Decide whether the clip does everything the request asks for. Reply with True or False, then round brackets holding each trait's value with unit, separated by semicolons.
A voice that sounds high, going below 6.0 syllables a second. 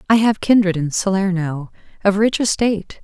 True (195 Hz; 5.2 syllables/s)